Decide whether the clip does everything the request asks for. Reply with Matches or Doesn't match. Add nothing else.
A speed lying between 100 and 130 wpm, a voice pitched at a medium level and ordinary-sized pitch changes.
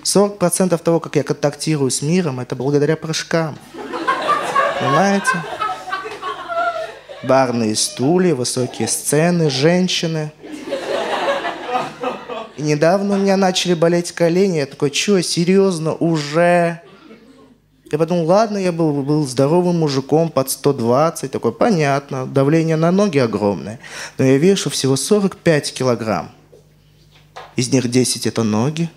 Matches